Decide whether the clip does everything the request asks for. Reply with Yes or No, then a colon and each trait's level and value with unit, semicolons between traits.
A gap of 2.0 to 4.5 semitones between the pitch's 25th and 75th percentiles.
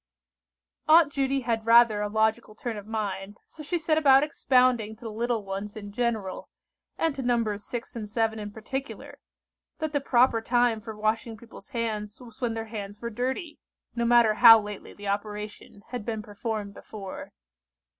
Yes: average, 2.7 semitones